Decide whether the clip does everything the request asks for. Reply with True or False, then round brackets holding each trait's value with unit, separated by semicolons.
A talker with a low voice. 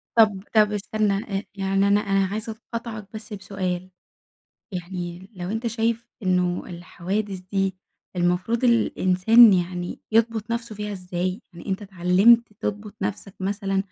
False (195 Hz)